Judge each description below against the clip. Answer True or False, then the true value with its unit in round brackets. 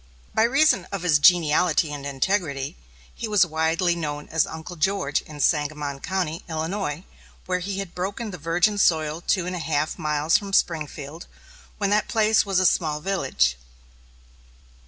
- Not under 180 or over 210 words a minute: False (155 wpm)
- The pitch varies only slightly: False (4.2 semitones)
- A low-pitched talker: False (165 Hz)